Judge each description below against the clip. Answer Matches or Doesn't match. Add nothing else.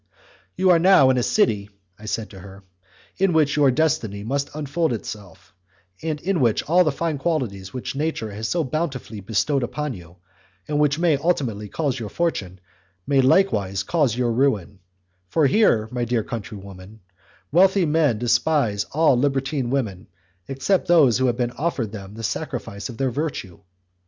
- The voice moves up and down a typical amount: Doesn't match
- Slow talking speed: Doesn't match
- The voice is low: Matches